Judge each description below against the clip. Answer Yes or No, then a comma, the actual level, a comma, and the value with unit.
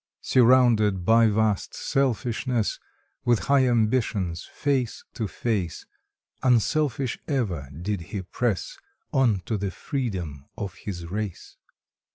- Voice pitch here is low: Yes, low, 110 Hz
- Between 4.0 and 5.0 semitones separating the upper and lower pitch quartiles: Yes, average, 4.7 semitones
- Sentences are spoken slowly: Yes, slow, 110 wpm